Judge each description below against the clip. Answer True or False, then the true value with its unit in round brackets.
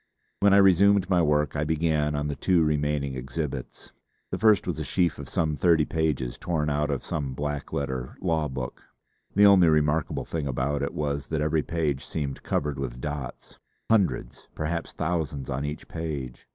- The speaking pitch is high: False (75 Hz)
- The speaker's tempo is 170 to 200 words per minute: True (180 wpm)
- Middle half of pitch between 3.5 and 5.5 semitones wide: False (2.8 semitones)